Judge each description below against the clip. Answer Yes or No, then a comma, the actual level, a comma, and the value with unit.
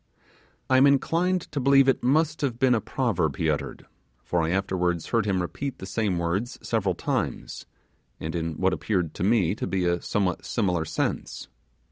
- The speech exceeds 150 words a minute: Yes, average, 180 wpm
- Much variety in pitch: Yes, wide, 6.9 semitones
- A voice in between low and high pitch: No, low, 100 Hz